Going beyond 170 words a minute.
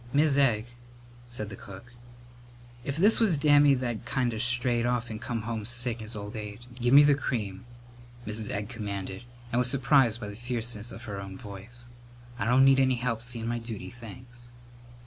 Yes: average, 195 wpm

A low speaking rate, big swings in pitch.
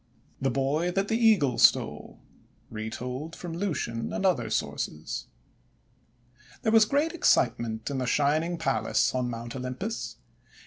Yes: slow, 130 wpm; wide, 7.8 semitones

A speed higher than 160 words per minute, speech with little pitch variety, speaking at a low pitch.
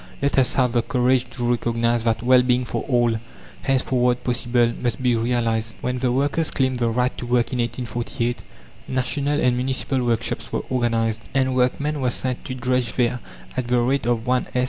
Yes: average, 185 wpm; narrow, 1.4 semitones; low, 125 Hz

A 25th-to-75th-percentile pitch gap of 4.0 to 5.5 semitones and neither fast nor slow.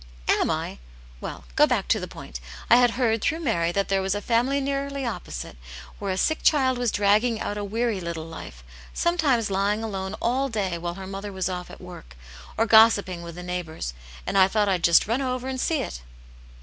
No: average, 5.2 semitones; fast, 210 wpm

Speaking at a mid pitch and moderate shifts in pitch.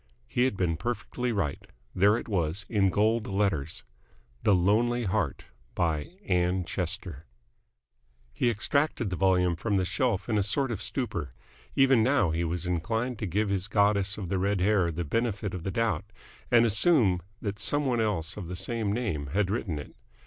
No: low, 100 Hz; average, 4.3 semitones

